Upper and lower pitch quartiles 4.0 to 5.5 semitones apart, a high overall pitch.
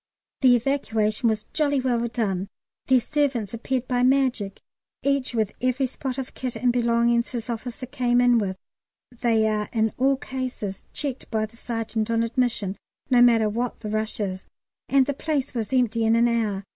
No: average, 2.8 semitones; high, 235 Hz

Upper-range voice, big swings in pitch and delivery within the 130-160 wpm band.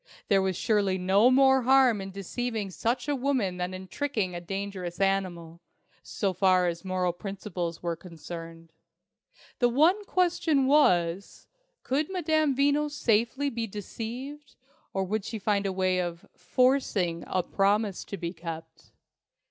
Yes: high, 200 Hz; wide, 6.1 semitones; average, 145 wpm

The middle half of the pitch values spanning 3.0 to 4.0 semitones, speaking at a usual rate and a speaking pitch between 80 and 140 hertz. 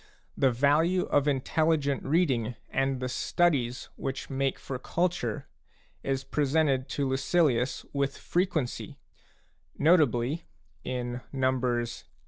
No: average, 3.5 semitones; slow, 105 wpm; low, 135 Hz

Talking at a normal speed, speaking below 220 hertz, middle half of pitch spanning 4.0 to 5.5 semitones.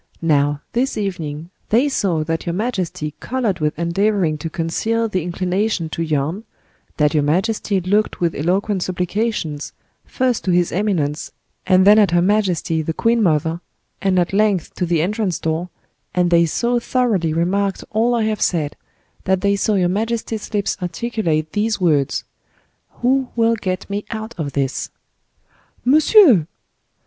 Yes: average, 155 wpm; medium, 185 Hz; average, 4.8 semitones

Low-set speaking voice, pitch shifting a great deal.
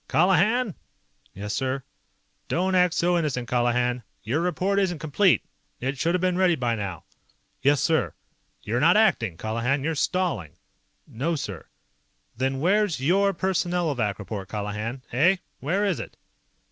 No: medium, 145 Hz; wide, 7.1 semitones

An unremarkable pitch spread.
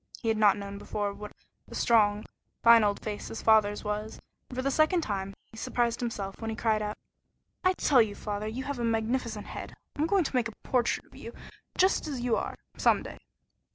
Yes: average, 3.1 semitones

